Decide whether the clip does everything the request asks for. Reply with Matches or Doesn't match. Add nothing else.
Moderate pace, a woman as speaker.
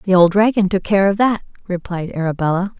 Matches